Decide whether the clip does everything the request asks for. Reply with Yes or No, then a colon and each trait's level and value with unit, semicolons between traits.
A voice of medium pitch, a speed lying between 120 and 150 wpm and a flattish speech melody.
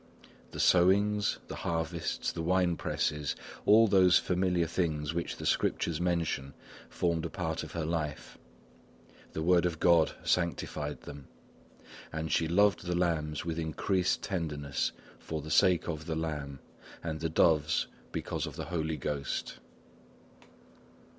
No: very low, 85 Hz; average, 140 wpm; narrow, 2.2 semitones